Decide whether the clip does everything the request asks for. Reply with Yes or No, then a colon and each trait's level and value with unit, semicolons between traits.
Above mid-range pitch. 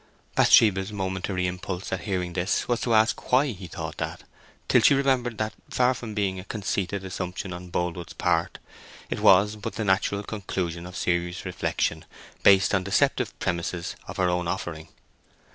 No: very low, 95 Hz